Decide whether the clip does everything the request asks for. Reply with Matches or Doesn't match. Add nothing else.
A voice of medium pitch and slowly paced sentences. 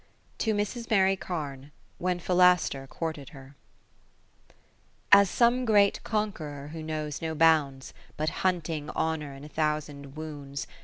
Matches